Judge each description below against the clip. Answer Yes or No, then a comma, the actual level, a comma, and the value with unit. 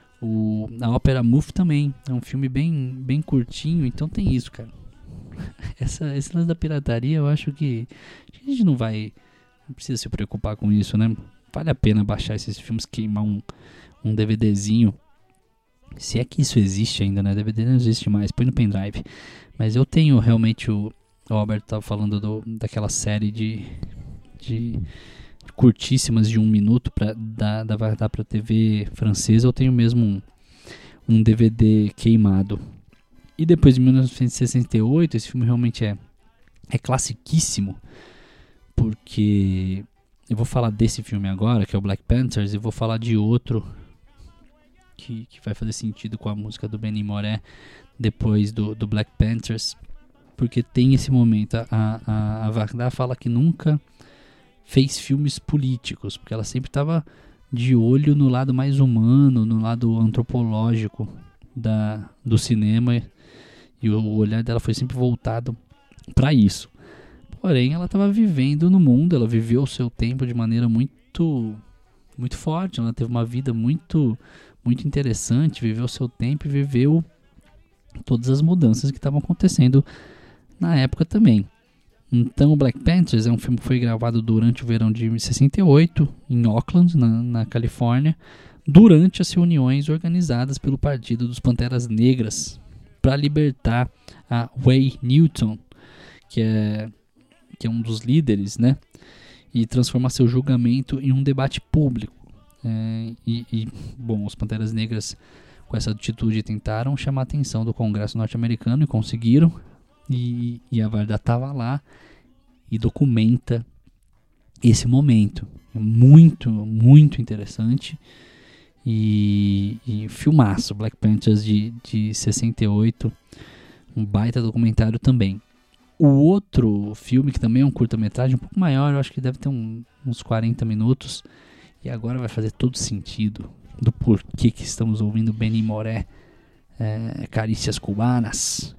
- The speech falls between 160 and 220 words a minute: No, average, 145 wpm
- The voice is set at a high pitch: No, low, 115 Hz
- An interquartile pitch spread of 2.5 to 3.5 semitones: Yes, average, 3.2 semitones